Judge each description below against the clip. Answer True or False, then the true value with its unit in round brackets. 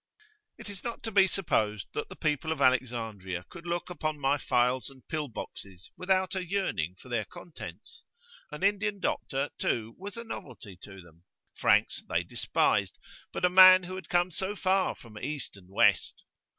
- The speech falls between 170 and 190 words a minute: True (175 wpm)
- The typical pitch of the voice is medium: True (150 Hz)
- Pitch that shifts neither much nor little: False (8.7 semitones)